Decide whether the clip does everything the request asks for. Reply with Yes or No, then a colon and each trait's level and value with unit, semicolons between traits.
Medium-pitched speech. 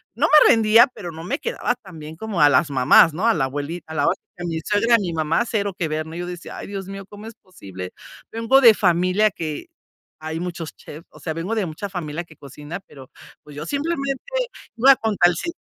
Yes: medium, 175 Hz